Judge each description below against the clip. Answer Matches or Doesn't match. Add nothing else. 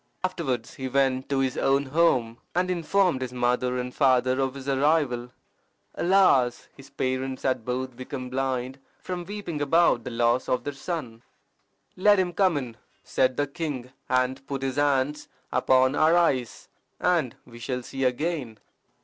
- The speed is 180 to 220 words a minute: Doesn't match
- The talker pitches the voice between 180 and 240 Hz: Doesn't match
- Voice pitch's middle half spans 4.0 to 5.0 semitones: Doesn't match